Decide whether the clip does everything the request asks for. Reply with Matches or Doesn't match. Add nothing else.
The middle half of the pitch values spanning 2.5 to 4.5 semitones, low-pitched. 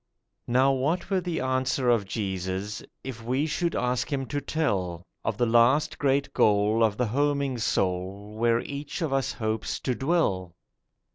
Doesn't match